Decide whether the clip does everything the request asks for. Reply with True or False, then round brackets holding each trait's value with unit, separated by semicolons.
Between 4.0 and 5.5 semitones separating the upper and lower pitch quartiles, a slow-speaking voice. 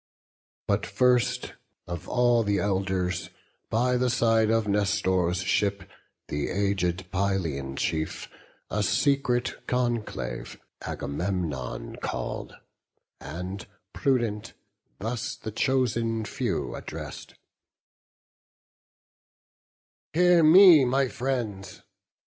True (5.0 semitones; 85 wpm)